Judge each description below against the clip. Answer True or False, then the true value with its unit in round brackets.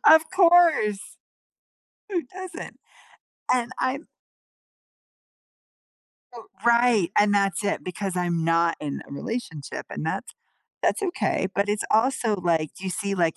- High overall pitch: True (205 Hz)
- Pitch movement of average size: False (6.5 semitones)